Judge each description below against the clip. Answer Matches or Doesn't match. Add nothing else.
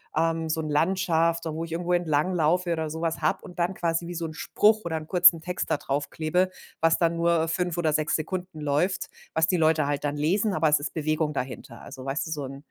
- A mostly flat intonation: Matches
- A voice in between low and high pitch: Matches